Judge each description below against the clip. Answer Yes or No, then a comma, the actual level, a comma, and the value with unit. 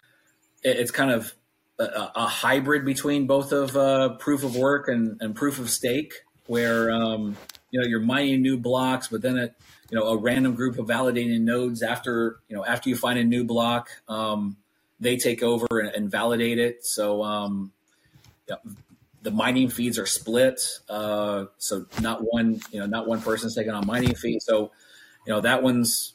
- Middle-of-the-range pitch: No, low, 120 Hz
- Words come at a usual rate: Yes, average, 185 wpm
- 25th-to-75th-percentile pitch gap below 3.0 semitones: Yes, narrow, 2.5 semitones